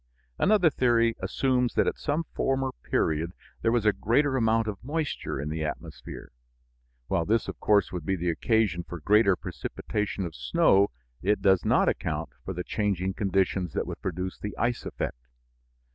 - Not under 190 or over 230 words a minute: No, average, 170 wpm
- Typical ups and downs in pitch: Yes, average, 4.8 semitones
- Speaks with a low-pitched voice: Yes, low, 100 Hz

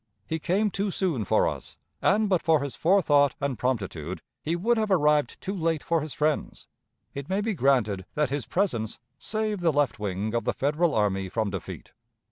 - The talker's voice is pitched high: No, medium, 150 Hz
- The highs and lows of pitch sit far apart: Yes, wide, 7.6 semitones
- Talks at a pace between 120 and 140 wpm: No, average, 190 wpm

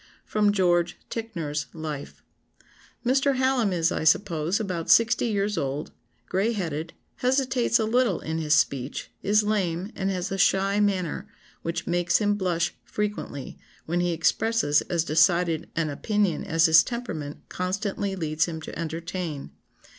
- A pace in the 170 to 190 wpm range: No, average, 145 wpm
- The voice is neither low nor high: Yes, medium, 180 Hz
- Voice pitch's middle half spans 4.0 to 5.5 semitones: Yes, average, 4.4 semitones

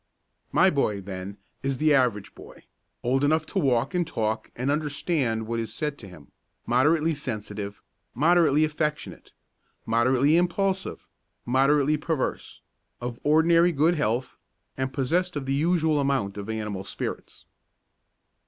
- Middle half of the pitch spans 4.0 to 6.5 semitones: Yes, average, 5.2 semitones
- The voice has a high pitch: No, medium, 140 Hz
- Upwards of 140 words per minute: No, slow, 135 wpm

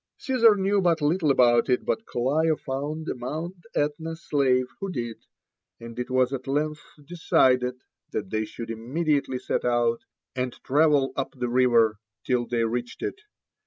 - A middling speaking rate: Yes, average, 160 wpm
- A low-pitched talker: Yes, low, 130 Hz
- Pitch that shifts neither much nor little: Yes, average, 4.4 semitones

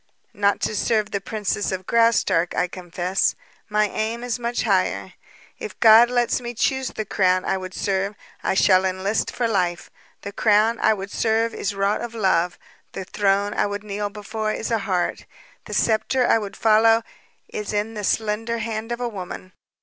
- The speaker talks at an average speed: Yes, average, 180 wpm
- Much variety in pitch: No, average, 2.7 semitones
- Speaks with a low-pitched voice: No, high, 210 Hz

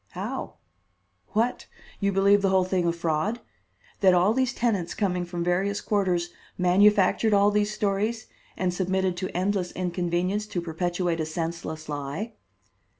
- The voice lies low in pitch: No, medium, 185 Hz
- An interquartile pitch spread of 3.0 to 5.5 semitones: No, narrow, 2.6 semitones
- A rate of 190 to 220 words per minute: No, average, 145 wpm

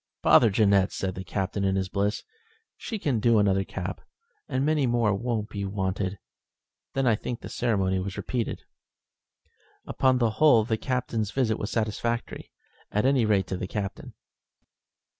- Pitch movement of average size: Yes, average, 3.6 semitones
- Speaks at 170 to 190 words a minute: No, average, 160 wpm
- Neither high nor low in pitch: No, low, 105 Hz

